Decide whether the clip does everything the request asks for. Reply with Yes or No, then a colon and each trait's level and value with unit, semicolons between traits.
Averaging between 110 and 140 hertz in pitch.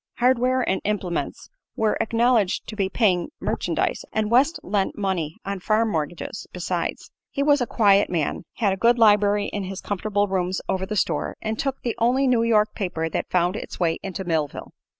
No: high, 205 Hz